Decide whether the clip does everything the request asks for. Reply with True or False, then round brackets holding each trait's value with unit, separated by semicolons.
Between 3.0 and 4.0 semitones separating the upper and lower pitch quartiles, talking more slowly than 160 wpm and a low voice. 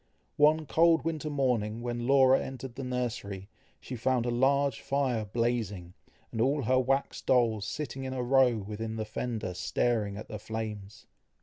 False (3.4 semitones; 165 wpm; 120 Hz)